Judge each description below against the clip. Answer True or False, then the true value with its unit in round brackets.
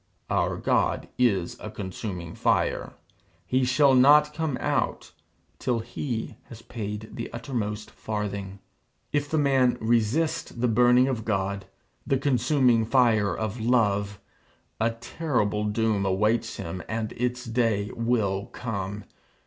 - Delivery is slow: True (125 wpm)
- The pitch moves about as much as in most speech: True (3.3 semitones)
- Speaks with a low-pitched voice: True (115 Hz)